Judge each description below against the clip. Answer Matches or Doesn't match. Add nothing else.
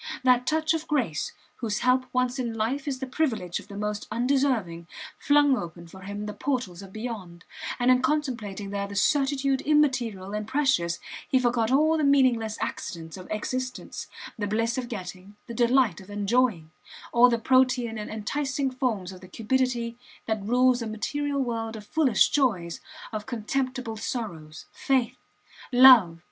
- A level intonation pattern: Doesn't match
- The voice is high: Matches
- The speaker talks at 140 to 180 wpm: Matches